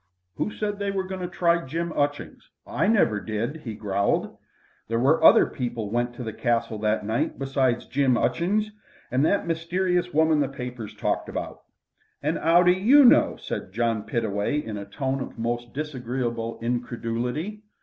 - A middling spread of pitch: No, wide, 6.5 semitones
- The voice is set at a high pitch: No, low, 130 Hz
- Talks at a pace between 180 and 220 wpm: No, average, 170 wpm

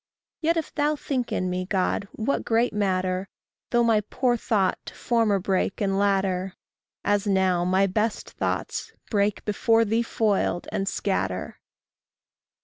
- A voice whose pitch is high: Yes, high, 200 Hz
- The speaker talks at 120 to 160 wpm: Yes, average, 140 wpm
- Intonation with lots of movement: No, average, 3.3 semitones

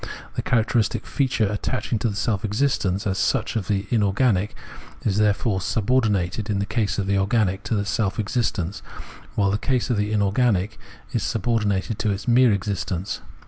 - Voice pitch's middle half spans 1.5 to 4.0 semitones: Yes, narrow, 2.6 semitones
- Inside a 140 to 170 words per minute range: No, average, 180 wpm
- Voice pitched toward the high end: No, low, 105 Hz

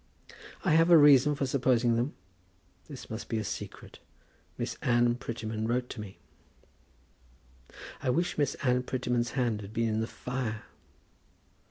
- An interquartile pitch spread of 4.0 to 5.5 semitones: No, average, 2.9 semitones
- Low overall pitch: Yes, low, 125 Hz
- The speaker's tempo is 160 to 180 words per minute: No, average, 150 wpm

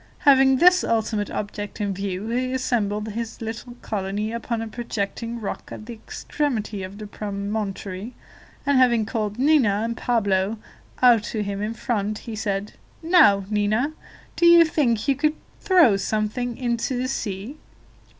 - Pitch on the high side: Yes, high, 225 Hz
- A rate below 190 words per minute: Yes, average, 150 wpm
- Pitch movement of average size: Yes, average, 3.4 semitones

